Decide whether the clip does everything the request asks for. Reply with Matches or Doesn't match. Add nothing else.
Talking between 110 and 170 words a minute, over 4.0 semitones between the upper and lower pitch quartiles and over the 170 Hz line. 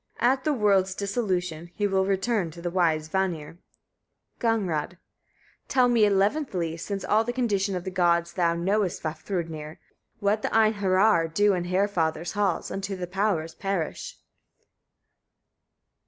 Doesn't match